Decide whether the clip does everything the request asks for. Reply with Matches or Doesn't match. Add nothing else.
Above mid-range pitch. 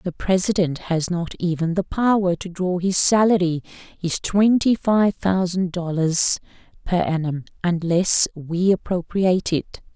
Doesn't match